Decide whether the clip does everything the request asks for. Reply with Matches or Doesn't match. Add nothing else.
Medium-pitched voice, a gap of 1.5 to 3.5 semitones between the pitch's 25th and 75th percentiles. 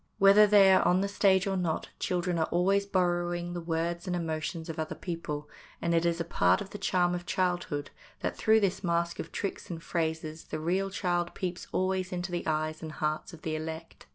Matches